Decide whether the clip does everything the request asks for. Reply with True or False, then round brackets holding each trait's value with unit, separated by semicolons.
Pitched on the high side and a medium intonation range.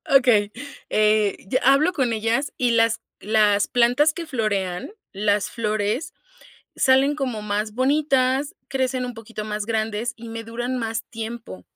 True (230 Hz; 3.4 semitones)